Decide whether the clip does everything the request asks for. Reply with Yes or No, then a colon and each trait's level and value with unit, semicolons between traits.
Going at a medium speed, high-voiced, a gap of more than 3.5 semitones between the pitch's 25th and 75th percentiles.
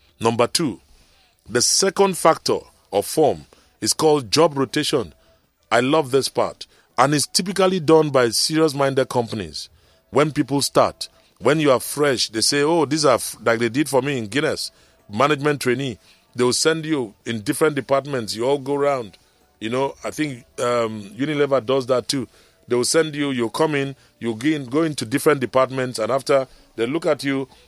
No: average, 180 wpm; low, 135 Hz; average, 4.0 semitones